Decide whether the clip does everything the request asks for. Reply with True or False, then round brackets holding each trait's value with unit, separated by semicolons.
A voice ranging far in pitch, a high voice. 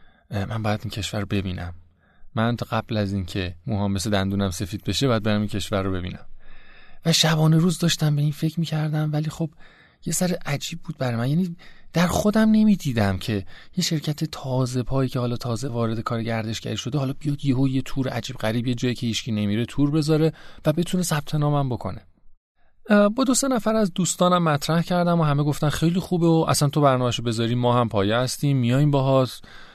False (6.3 semitones; 135 Hz)